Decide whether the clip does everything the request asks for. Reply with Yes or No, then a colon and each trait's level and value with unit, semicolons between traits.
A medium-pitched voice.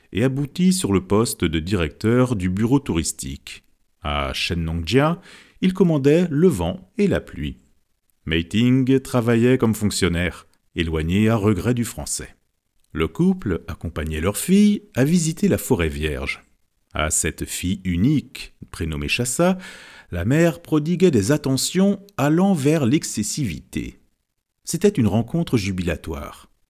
No: low, 110 Hz